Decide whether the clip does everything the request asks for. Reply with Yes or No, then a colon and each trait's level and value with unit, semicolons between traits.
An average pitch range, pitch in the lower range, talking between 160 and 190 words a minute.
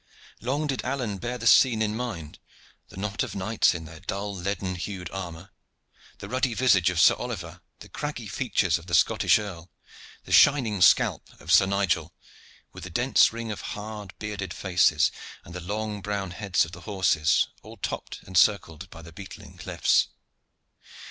Yes: average, 3.4 semitones; low, 100 Hz; average, 175 wpm